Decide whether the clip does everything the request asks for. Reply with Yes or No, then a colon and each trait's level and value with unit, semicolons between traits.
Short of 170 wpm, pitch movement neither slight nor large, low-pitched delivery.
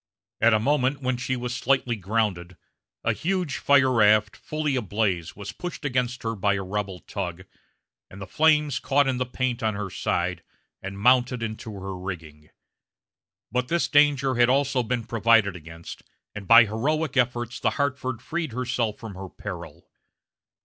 Yes: average, 160 wpm; average, 4.5 semitones; low, 115 Hz